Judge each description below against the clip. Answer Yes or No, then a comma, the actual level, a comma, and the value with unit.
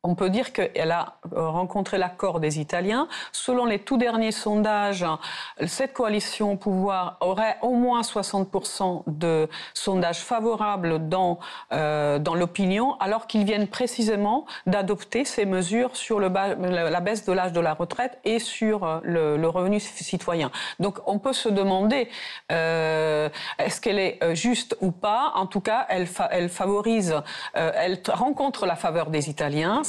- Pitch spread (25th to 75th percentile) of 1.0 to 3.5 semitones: No, average, 4.5 semitones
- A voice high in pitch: Yes, high, 195 Hz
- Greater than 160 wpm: No, average, 155 wpm